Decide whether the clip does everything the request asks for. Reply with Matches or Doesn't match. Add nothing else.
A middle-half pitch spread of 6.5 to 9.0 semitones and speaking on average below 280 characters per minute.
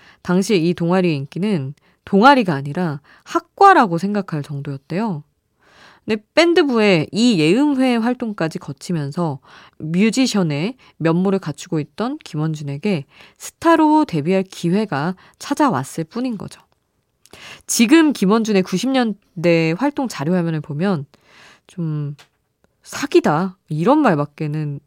Matches